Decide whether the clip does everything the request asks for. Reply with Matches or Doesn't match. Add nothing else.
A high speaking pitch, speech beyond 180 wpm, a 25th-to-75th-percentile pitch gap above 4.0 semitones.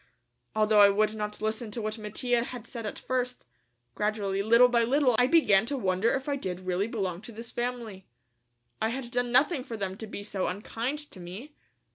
Doesn't match